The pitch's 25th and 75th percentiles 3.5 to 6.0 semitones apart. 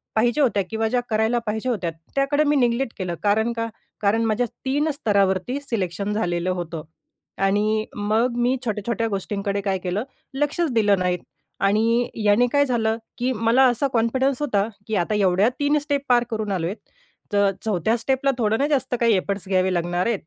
Yes: average, 3.8 semitones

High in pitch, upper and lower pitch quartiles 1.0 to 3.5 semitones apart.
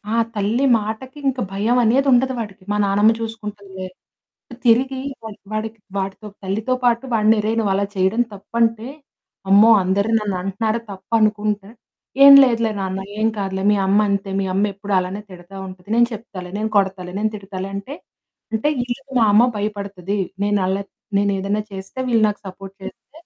Yes: high, 205 Hz; narrow, 2.5 semitones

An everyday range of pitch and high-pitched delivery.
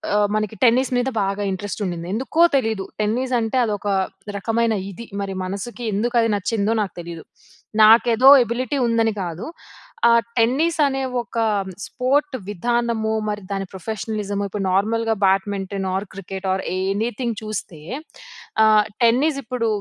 Yes: average, 3.2 semitones; high, 220 Hz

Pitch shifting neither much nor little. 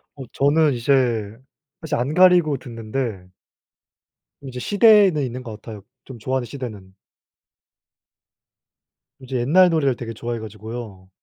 Yes: average, 4.5 semitones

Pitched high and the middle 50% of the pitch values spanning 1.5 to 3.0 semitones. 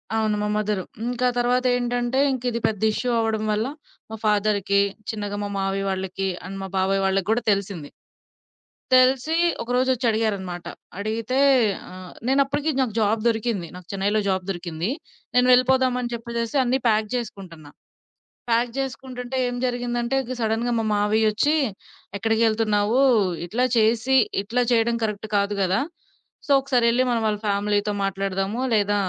No: high, 220 Hz; average, 3.4 semitones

